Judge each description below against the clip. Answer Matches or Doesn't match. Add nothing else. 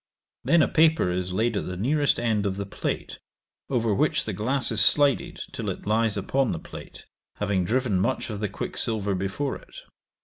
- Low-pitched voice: Matches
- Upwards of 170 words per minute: Matches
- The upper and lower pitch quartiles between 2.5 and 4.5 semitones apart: Doesn't match